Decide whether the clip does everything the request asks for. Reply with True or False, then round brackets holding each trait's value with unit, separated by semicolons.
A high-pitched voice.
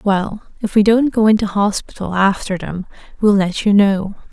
True (205 Hz)